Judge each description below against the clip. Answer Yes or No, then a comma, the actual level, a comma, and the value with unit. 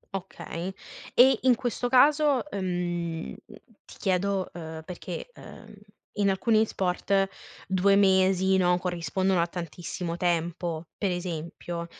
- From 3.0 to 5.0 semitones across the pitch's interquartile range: No, narrow, 2.4 semitones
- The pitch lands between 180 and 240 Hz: Yes, medium, 185 Hz